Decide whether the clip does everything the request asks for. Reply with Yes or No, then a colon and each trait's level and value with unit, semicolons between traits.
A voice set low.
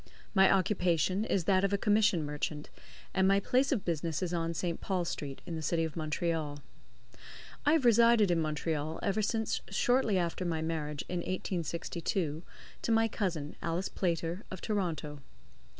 No: medium, 175 Hz